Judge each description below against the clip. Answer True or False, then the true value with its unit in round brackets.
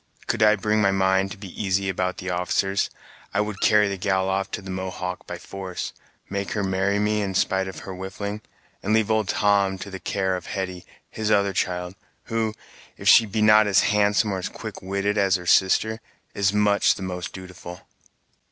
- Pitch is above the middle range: False (95 Hz)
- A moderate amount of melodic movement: False (1.7 semitones)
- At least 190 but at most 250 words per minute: True (200 wpm)